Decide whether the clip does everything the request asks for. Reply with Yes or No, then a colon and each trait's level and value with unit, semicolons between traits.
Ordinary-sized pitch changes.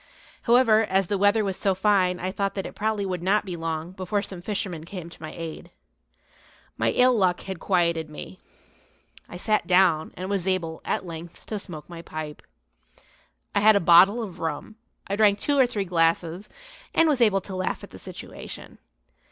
Yes: average, 3.4 semitones